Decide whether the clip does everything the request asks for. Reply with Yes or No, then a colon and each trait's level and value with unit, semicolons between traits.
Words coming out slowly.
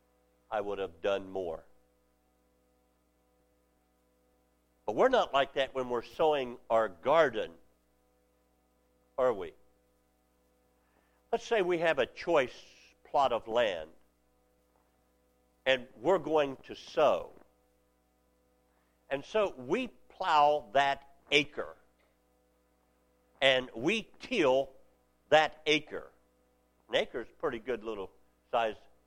Yes: slow, 100 wpm